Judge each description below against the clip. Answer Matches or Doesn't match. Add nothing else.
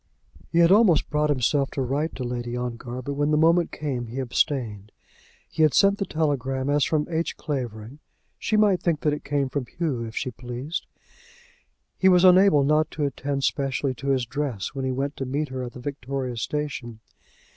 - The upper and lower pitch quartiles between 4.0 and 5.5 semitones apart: Doesn't match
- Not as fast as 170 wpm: Doesn't match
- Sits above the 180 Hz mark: Doesn't match